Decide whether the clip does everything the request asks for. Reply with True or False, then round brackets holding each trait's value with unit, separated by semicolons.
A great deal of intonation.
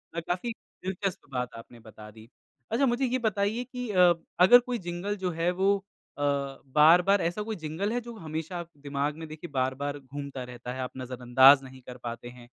True (7.4 semitones)